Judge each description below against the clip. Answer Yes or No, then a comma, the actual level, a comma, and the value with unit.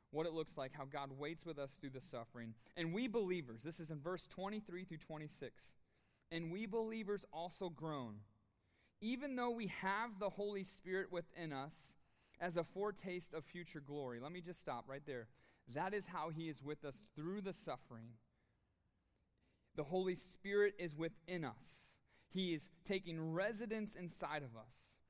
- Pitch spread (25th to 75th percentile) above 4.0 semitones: Yes, average, 5.3 semitones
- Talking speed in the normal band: Yes, average, 170 wpm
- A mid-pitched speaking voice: Yes, medium, 165 Hz